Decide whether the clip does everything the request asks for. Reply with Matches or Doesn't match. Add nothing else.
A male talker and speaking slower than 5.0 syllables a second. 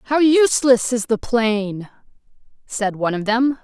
Doesn't match